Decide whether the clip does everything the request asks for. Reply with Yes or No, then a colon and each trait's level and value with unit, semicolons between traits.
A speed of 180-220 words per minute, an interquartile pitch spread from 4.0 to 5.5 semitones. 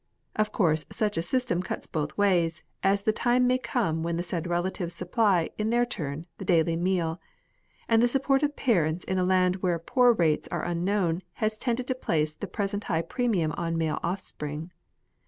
Yes: average, 190 wpm; average, 4.7 semitones